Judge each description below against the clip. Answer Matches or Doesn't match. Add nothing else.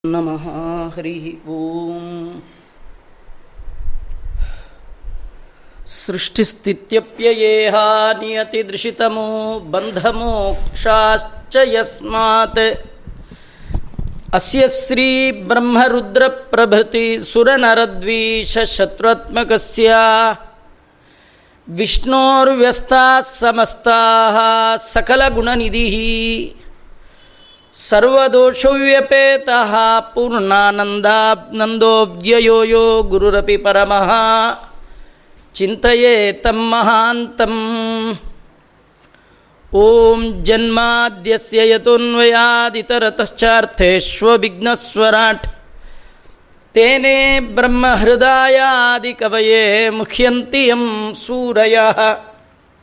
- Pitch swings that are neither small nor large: Doesn't match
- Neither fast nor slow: Doesn't match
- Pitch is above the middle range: Matches